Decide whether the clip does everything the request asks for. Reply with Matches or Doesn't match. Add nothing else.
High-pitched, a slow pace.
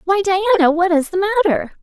Doesn't match